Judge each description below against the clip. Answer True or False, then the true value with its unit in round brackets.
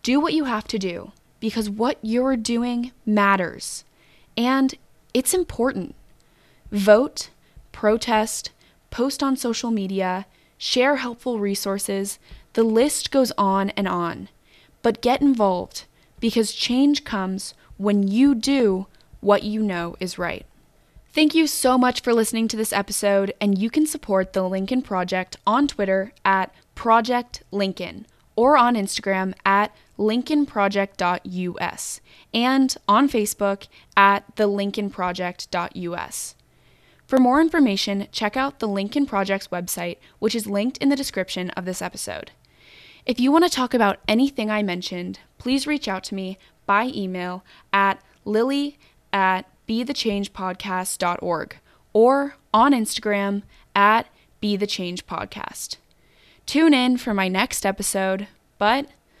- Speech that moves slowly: True (130 wpm)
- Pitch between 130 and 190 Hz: False (210 Hz)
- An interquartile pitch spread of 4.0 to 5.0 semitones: True (4.4 semitones)